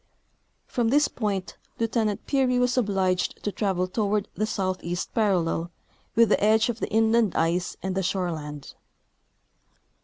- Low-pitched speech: No, high, 205 Hz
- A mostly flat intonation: No, average, 3.6 semitones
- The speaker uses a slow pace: No, average, 150 wpm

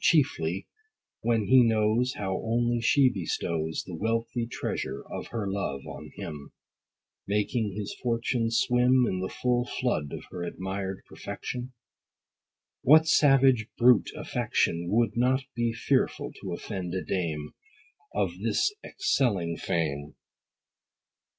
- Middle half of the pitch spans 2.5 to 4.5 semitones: No, average, 5.1 semitones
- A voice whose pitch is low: Yes, low, 115 Hz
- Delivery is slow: Yes, slow, 125 wpm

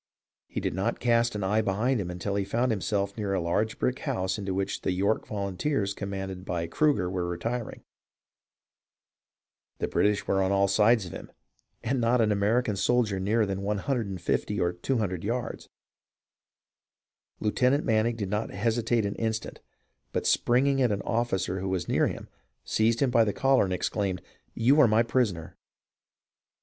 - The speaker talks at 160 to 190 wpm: Yes, average, 170 wpm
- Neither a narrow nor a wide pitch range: Yes, average, 3.4 semitones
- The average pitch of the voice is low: Yes, low, 105 Hz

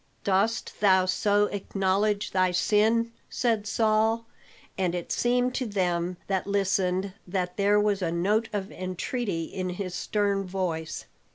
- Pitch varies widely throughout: No, narrow, 2.5 semitones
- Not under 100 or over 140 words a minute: Yes, slow, 135 wpm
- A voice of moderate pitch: No, high, 195 Hz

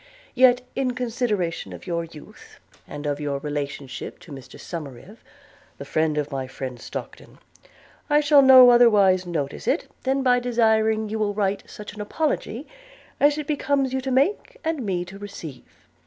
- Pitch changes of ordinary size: No, wide, 8.3 semitones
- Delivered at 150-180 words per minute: Yes, average, 165 wpm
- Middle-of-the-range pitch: No, high, 210 Hz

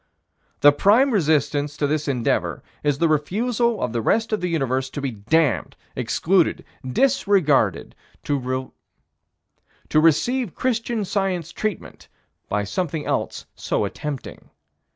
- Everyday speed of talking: No, slow, 120 wpm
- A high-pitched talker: No, medium, 155 Hz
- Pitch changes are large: Yes, wide, 7.0 semitones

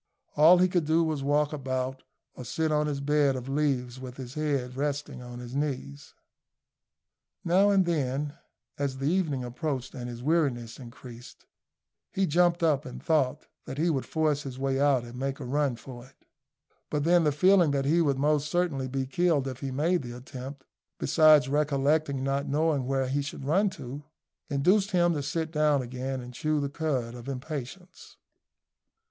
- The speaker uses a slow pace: No, average, 180 wpm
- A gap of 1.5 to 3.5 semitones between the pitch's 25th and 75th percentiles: Yes, average, 3.0 semitones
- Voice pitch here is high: No, medium, 140 Hz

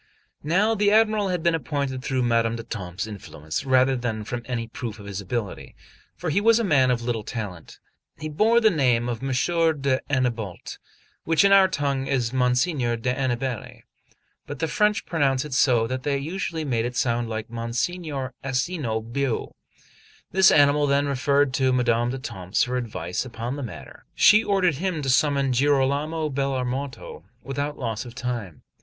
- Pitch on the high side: No, low, 130 Hz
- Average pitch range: Yes, average, 4.1 semitones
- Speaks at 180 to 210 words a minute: No, average, 165 wpm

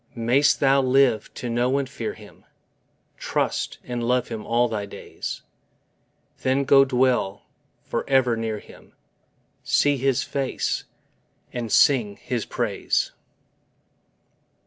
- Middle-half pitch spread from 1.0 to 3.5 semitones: Yes, average, 2.8 semitones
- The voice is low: Yes, low, 125 Hz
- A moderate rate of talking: No, slow, 120 wpm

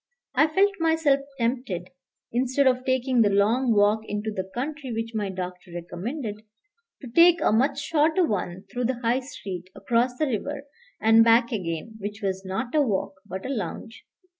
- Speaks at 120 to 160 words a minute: No, average, 170 wpm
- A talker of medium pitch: No, high, 230 Hz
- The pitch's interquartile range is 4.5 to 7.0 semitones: Yes, average, 4.8 semitones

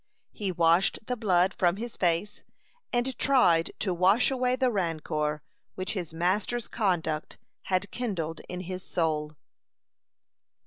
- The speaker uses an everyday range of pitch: Yes, average, 4.7 semitones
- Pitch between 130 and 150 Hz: No, medium, 185 Hz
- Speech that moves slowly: Yes, slow, 130 wpm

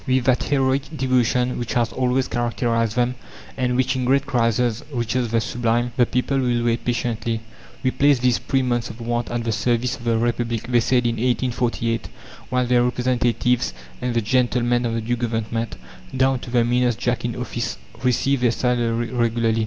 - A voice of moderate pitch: No, low, 120 Hz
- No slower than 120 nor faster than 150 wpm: No, average, 185 wpm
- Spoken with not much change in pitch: Yes, narrow, 1.4 semitones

